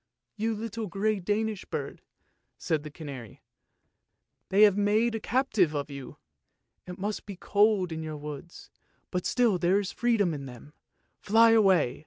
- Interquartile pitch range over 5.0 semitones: Yes, wide, 5.5 semitones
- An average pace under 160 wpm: No, average, 175 wpm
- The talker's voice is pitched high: Yes, high, 195 Hz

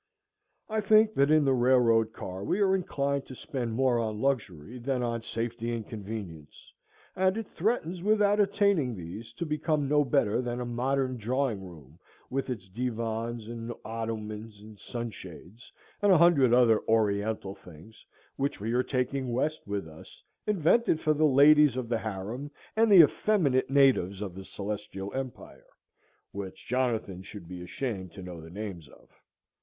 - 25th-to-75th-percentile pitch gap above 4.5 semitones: Yes, average, 5.2 semitones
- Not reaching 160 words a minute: No, average, 165 wpm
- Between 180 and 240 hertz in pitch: No, low, 120 Hz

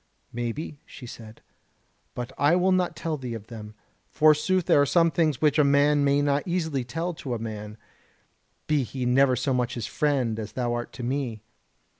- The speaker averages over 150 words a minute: Yes, average, 190 wpm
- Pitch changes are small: No, average, 4.2 semitones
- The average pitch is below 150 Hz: Yes, medium, 140 Hz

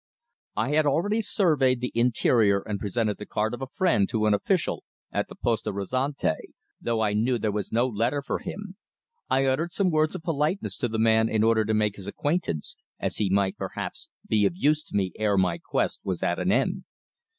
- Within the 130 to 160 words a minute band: No, fast, 205 wpm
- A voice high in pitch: No, low, 115 Hz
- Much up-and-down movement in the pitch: Yes, wide, 5.9 semitones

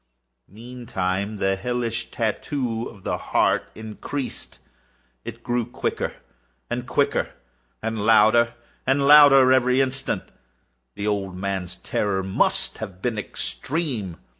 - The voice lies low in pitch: Yes, low, 115 Hz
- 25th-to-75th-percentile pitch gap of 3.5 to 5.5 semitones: Yes, average, 4.1 semitones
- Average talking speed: No, slow, 115 wpm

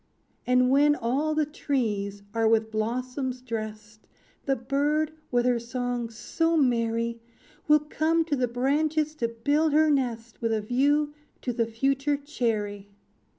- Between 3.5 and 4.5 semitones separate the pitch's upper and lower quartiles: Yes, average, 4.2 semitones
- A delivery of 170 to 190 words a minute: No, average, 145 wpm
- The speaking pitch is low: No, very high, 250 Hz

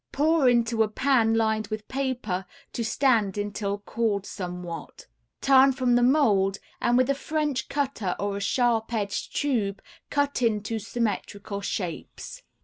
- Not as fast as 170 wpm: Yes, average, 140 wpm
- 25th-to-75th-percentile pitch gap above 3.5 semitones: Yes, average, 4.4 semitones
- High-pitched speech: Yes, high, 225 Hz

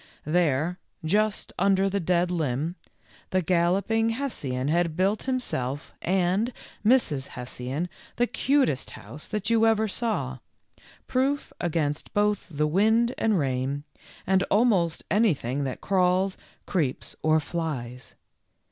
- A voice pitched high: No, medium, 180 Hz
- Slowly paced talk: Yes, slow, 120 wpm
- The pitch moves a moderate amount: No, wide, 6.4 semitones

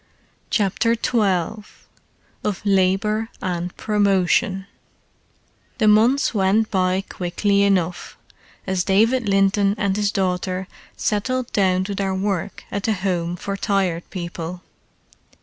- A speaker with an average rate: No, slow, 115 wpm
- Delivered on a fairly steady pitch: Yes, narrow, 2.3 semitones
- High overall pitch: Yes, high, 195 Hz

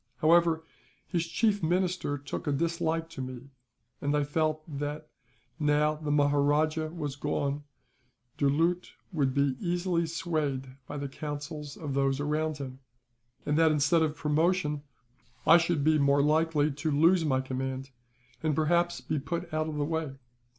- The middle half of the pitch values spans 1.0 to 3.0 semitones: Yes, narrow, 2.4 semitones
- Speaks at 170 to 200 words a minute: No, average, 150 wpm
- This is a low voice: No, medium, 150 Hz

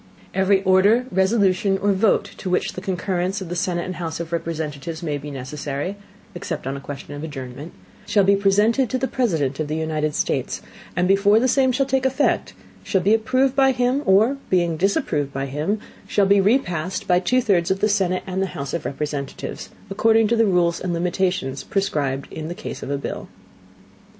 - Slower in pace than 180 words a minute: No, average, 195 wpm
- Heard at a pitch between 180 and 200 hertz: Yes, medium, 185 Hz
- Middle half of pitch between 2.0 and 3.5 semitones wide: No, average, 4.7 semitones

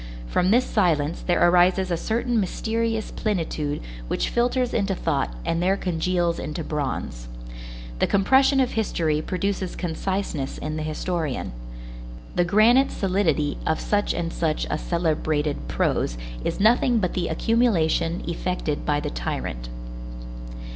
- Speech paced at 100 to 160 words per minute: Yes, slow, 135 wpm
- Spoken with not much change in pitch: No, average, 4.9 semitones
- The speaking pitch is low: No, medium, 175 Hz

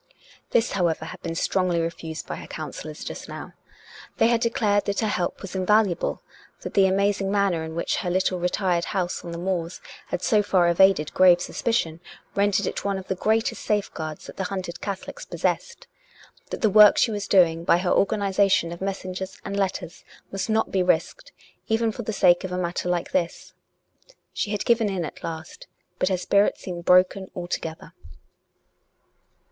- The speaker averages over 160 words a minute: Yes, average, 185 wpm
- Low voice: No, high, 190 Hz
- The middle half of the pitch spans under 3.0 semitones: Yes, narrow, 2.6 semitones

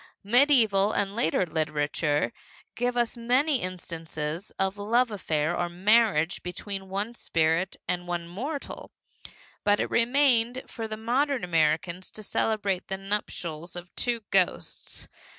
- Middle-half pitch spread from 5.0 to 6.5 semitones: Yes, average, 5.3 semitones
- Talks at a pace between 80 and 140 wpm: Yes, slow, 135 wpm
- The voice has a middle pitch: No, high, 195 Hz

